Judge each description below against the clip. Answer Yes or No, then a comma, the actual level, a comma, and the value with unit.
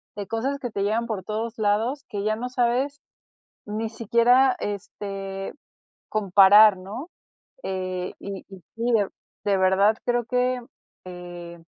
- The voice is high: Yes, high, 215 Hz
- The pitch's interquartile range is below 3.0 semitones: No, average, 3.7 semitones